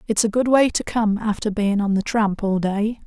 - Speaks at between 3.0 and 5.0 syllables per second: Yes, 4.9 syllables/s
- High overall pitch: Yes, high, 215 Hz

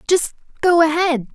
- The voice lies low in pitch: No, very high, 320 Hz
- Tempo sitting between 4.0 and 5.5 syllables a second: Yes, 5.1 syllables/s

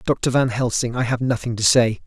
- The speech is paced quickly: Yes, fast, 230 wpm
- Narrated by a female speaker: No, male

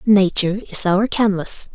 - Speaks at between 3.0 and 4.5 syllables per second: Yes, 4.4 syllables/s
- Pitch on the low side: No, high, 195 Hz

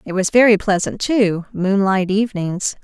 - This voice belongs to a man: No, female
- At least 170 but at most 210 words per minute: No, average, 150 wpm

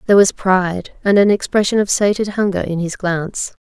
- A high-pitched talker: Yes, high, 195 Hz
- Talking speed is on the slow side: No, average, 200 wpm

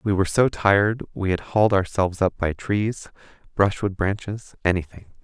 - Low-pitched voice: Yes, low, 100 Hz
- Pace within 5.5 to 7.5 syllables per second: No, 5.3 syllables/s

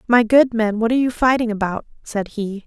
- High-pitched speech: Yes, high, 225 Hz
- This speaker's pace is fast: Yes, fast, 225 wpm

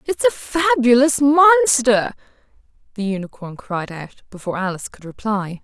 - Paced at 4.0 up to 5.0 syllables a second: Yes, 4.7 syllables/s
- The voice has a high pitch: Yes, high, 240 Hz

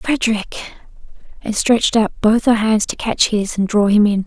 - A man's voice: No, female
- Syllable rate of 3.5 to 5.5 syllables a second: Yes, 4.7 syllables/s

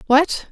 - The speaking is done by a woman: Yes, female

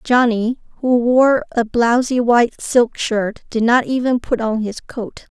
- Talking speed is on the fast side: No, average, 170 wpm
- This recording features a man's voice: No, female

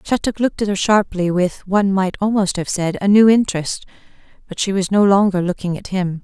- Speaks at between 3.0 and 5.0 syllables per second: No, 5.7 syllables/s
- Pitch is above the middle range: Yes, high, 195 Hz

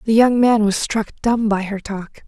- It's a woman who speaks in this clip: Yes, female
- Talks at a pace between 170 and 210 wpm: No, fast, 235 wpm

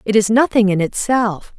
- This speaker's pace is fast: No, average, 190 wpm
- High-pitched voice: Yes, high, 215 Hz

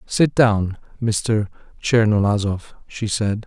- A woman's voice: No, male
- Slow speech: Yes, slow, 105 wpm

